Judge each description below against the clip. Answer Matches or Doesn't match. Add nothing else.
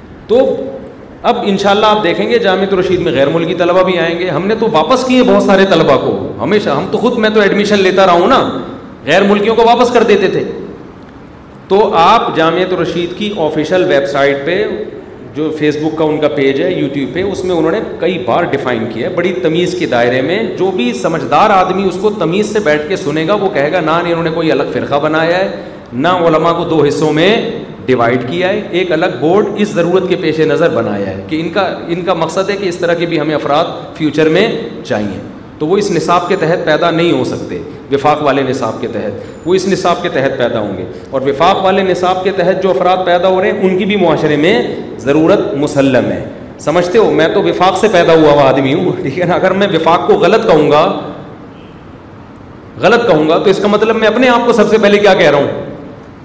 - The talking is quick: Matches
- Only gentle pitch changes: Doesn't match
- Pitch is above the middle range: Doesn't match